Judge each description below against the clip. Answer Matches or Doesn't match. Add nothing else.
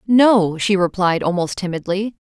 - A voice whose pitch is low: Doesn't match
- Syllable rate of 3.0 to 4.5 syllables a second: Matches